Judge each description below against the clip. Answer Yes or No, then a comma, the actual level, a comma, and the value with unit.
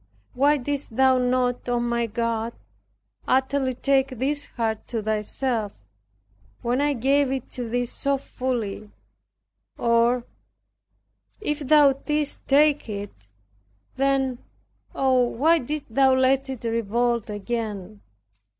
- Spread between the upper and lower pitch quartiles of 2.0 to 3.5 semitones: Yes, average, 2.8 semitones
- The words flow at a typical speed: No, slow, 115 wpm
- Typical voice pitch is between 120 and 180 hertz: No, very high, 250 Hz